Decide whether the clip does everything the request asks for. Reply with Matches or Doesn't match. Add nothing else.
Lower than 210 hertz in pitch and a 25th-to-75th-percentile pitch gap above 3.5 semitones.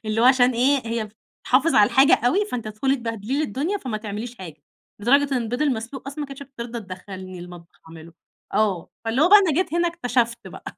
Doesn't match